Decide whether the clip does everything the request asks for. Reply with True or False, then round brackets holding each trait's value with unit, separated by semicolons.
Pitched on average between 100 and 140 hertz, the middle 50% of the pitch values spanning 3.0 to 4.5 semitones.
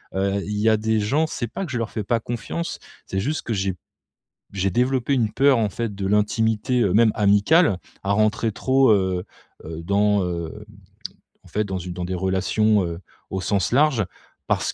True (105 Hz; 3.4 semitones)